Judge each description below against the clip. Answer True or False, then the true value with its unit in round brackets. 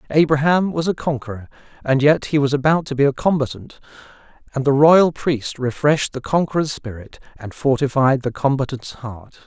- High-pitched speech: False (140 Hz)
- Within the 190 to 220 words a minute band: False (165 wpm)